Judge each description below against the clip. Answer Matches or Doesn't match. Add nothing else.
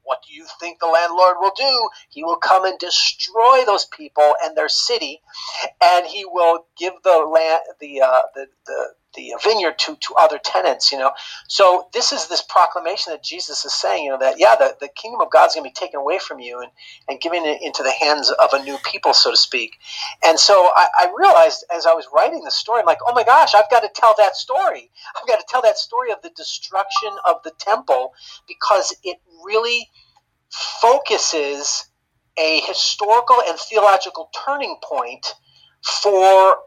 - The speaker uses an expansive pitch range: Matches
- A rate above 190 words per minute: Matches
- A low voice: Doesn't match